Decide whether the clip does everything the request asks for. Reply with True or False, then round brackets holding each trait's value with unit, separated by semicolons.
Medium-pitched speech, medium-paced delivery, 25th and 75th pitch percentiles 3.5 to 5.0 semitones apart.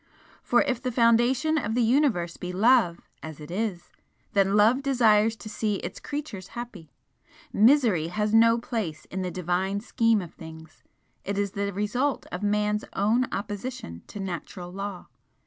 False (210 Hz; 160 wpm; 4.3 semitones)